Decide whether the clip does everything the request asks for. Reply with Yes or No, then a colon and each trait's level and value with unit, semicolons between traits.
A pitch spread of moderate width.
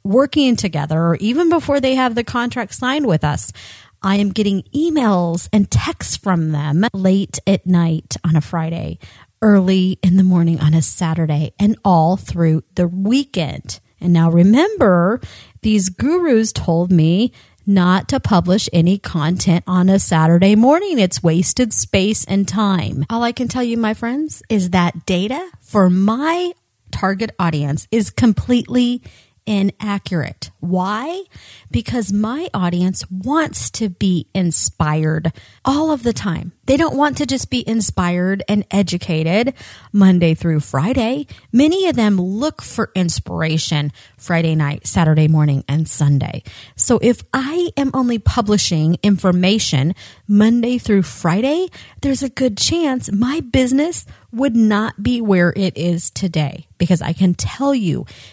No: wide, 6.2 semitones